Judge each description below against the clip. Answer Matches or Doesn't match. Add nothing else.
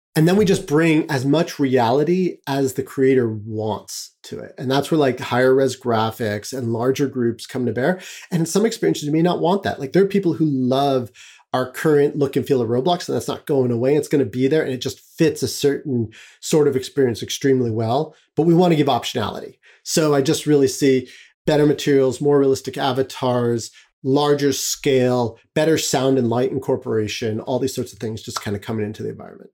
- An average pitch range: Matches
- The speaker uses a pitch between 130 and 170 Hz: Matches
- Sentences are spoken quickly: Matches